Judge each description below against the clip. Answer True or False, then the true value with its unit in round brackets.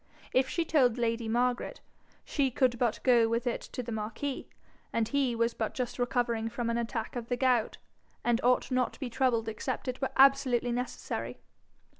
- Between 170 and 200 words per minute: True (185 wpm)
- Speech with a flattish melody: True (1.9 semitones)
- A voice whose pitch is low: False (245 Hz)